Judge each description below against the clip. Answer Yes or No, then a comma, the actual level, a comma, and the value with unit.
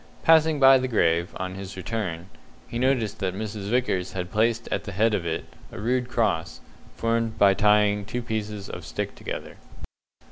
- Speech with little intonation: No, average, 3.5 semitones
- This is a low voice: Yes, low, 105 Hz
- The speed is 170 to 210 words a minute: Yes, average, 175 wpm